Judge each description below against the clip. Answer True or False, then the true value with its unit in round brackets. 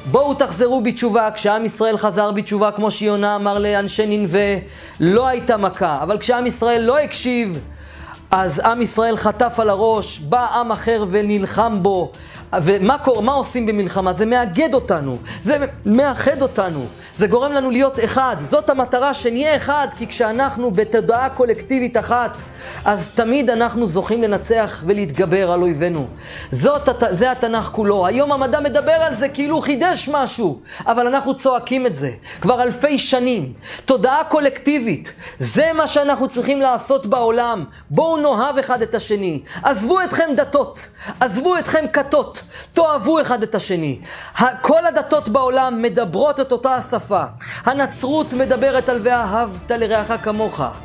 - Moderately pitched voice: False (240 Hz)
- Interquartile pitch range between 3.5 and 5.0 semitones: True (4.5 semitones)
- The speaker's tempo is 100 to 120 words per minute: False (140 wpm)